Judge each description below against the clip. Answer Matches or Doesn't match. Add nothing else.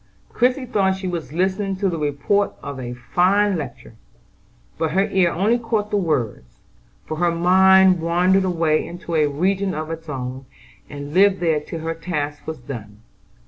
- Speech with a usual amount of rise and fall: Matches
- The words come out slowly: Doesn't match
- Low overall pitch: Doesn't match